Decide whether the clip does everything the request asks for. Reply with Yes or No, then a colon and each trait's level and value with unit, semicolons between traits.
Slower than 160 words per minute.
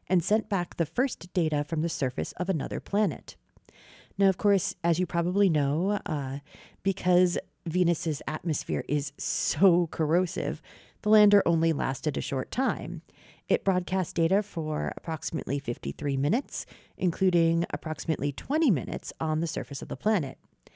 Yes: average, 145 wpm